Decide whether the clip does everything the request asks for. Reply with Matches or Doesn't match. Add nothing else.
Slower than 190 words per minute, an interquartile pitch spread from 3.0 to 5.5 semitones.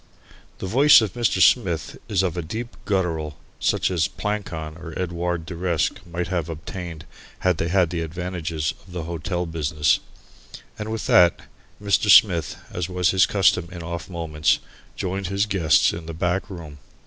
Doesn't match